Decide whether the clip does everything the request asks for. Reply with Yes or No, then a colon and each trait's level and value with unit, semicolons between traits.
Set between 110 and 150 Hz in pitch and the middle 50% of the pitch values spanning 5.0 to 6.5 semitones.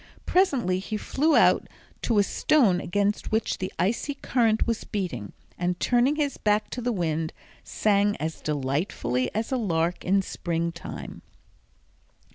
No: high, 200 Hz; wide, 5.5 semitones